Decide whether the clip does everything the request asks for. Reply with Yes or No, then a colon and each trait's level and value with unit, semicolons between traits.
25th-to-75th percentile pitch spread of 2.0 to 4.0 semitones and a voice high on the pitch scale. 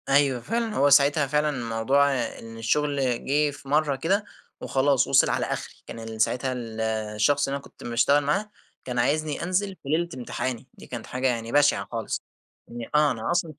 No: average, 3.6 semitones; medium, 140 Hz